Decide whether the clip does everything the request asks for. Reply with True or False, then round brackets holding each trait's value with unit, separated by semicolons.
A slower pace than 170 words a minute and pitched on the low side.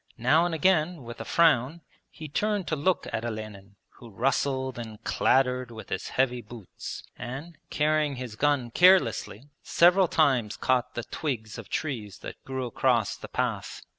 True (160 wpm; 130 Hz)